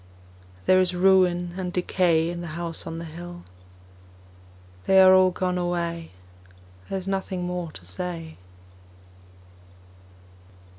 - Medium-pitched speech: Yes, medium, 175 Hz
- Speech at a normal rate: No, slow, 120 wpm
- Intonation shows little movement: Yes, narrow, 1.6 semitones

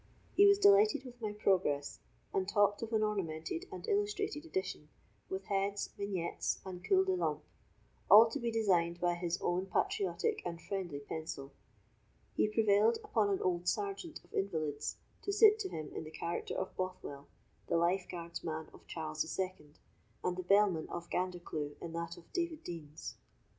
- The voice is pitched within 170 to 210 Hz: Yes, high, 190 Hz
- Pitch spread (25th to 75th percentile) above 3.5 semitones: Yes, wide, 5.4 semitones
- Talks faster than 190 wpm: No, average, 170 wpm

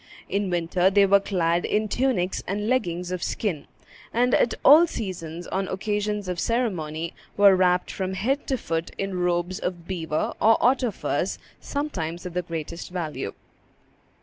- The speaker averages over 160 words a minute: No, average, 155 wpm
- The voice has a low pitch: No, medium, 185 Hz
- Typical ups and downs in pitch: Yes, average, 3.4 semitones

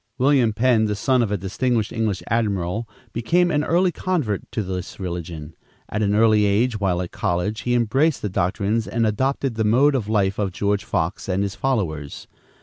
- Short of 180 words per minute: No, average, 185 wpm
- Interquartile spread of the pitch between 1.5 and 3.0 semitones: No, average, 4.0 semitones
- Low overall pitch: Yes, low, 105 Hz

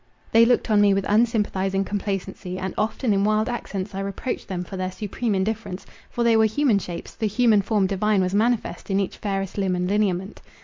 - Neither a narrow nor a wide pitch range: No, narrow, 2.3 semitones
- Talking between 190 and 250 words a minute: Yes, average, 200 wpm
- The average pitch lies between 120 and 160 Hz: No, high, 200 Hz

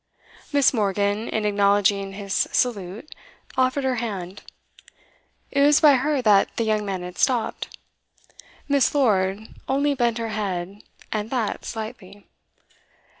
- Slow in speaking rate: Yes, slow, 125 wpm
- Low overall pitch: No, high, 215 Hz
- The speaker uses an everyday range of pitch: Yes, average, 4.3 semitones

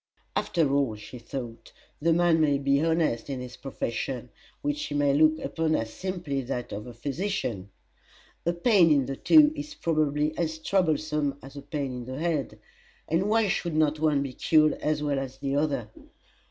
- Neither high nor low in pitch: Yes, medium, 150 Hz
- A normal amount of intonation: Yes, average, 3.4 semitones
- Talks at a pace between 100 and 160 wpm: No, average, 180 wpm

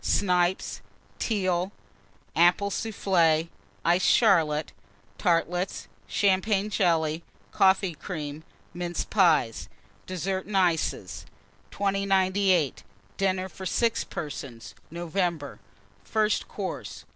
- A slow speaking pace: Yes, slow, 85 wpm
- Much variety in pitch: No, average, 3.1 semitones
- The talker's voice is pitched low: No, medium, 180 Hz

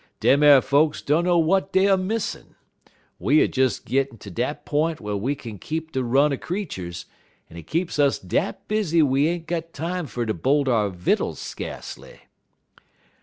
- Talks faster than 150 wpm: Yes, average, 175 wpm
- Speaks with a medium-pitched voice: Yes, medium, 145 Hz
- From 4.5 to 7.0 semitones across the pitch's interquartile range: Yes, average, 5.1 semitones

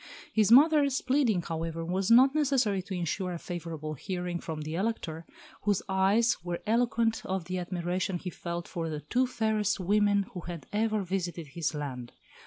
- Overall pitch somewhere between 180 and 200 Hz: Yes, medium, 185 Hz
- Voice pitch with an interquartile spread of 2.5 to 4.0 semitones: No, average, 4.4 semitones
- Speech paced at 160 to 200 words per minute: Yes, average, 170 wpm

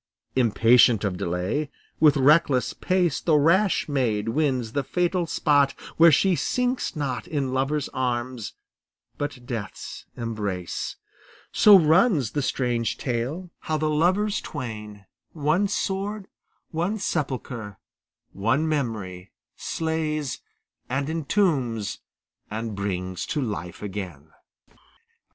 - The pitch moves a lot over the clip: Yes, wide, 6.2 semitones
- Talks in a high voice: No, low, 135 Hz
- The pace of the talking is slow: Yes, slow, 110 wpm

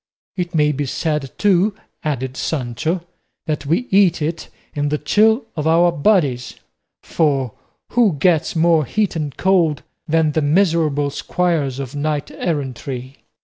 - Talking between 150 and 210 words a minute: No, average, 140 wpm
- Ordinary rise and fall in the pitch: Yes, average, 3.4 semitones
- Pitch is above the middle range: No, medium, 155 Hz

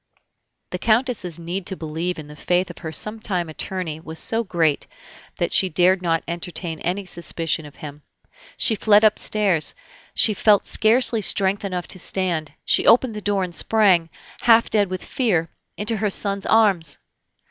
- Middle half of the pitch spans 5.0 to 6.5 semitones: No, average, 4.2 semitones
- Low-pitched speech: No, medium, 185 Hz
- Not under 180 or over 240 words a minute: No, average, 165 wpm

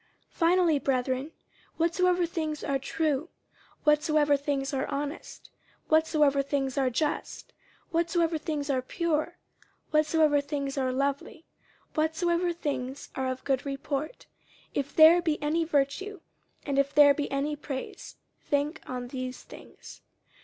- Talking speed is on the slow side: Yes, slow, 130 wpm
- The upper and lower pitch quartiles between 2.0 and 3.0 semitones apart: Yes, average, 2.7 semitones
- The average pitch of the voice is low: No, very high, 295 Hz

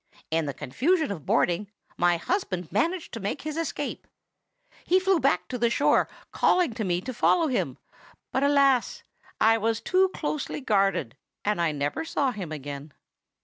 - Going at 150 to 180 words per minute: Yes, average, 165 wpm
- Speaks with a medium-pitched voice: No, high, 225 Hz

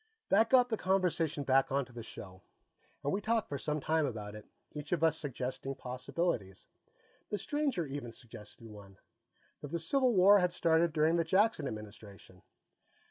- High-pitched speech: No, medium, 150 Hz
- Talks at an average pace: Yes, average, 165 wpm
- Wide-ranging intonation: Yes, wide, 7.0 semitones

